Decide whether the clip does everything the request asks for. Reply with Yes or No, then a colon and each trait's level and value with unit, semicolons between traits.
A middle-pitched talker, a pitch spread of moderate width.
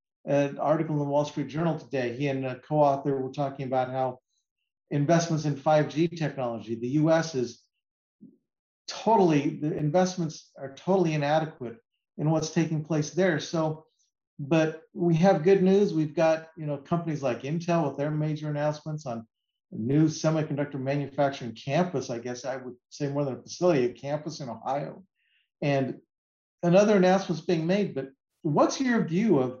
Yes: medium, 150 Hz; average, 3.5 semitones